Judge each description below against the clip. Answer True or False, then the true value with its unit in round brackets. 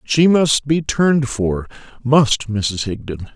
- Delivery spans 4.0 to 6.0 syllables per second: False (6.3 syllables/s)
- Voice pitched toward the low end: True (130 Hz)